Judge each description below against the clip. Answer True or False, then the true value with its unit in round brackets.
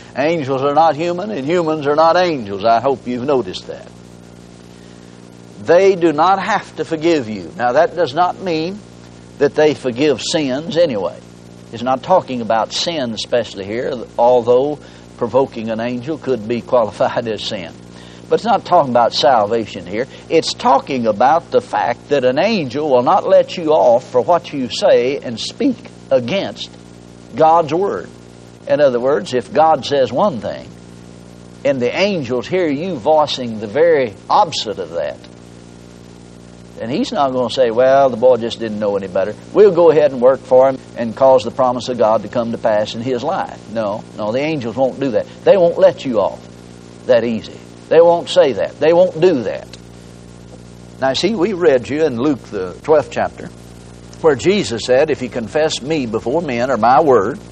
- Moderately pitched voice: False (120 Hz)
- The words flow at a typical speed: True (180 wpm)